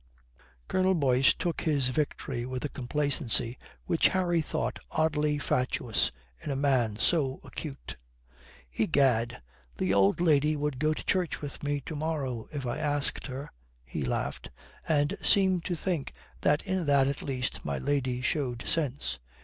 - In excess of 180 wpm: No, average, 150 wpm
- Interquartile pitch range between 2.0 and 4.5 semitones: Yes, average, 3.4 semitones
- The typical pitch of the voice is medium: Yes, medium, 145 Hz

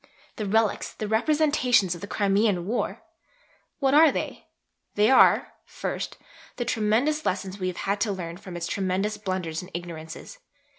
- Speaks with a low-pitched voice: No, high, 205 Hz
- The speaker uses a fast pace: No, average, 155 wpm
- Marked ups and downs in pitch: No, average, 4.2 semitones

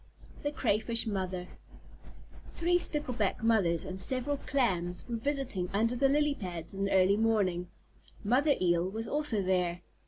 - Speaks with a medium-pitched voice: No, high, 215 Hz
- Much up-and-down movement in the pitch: Yes, wide, 6.3 semitones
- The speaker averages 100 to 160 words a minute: Yes, average, 145 wpm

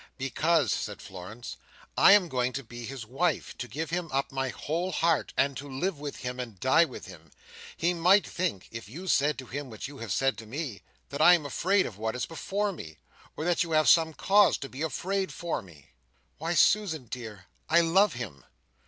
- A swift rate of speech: Yes, fast, 210 wpm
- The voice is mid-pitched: Yes, medium, 145 Hz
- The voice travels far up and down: Yes, wide, 5.9 semitones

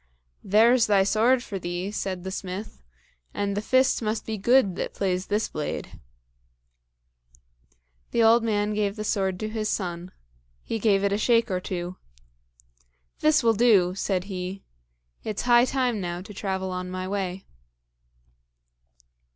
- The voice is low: No, high, 200 Hz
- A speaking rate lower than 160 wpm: Yes, average, 150 wpm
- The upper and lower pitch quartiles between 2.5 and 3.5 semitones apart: Yes, average, 3.2 semitones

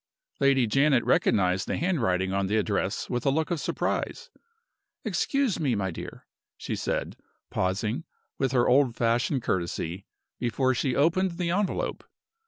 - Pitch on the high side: No, low, 125 Hz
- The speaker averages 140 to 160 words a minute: Yes, average, 145 wpm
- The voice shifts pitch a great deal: Yes, wide, 7.3 semitones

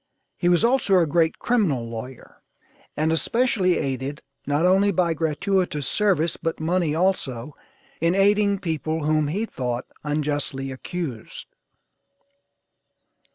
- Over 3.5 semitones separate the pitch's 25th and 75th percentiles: Yes, average, 4.5 semitones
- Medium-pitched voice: Yes, medium, 160 Hz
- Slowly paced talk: Yes, slow, 115 wpm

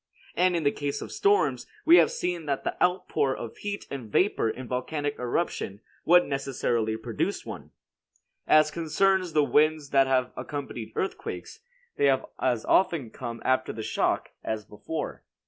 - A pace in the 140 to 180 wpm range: Yes, average, 165 wpm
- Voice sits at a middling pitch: Yes, medium, 145 Hz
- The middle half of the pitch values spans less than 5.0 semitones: No, wide, 5.6 semitones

